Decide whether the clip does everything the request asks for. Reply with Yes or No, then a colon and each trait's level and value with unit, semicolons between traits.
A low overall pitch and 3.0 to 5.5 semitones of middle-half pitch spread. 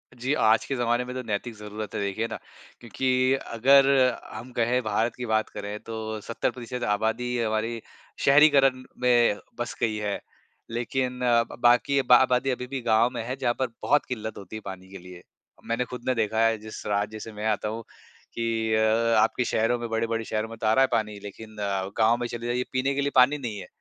No: low, 115 Hz; narrow, 2.4 semitones